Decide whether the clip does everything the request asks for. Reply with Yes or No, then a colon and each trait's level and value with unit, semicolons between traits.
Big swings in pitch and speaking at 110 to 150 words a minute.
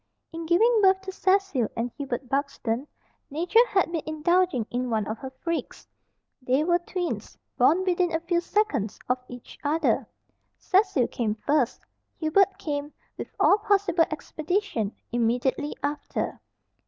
Yes: wide, 6.4 semitones; average, 140 wpm